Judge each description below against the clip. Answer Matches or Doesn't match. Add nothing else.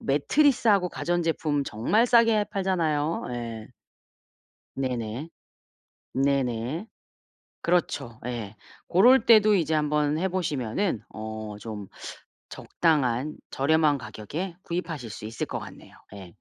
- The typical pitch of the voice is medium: Matches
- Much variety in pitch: Matches